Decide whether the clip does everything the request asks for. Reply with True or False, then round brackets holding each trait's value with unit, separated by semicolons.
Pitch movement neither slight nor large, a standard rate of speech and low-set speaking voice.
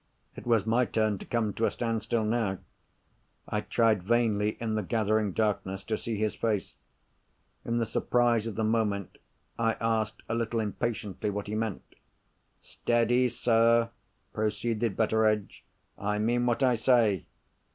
False (1.7 semitones; 150 wpm; 110 Hz)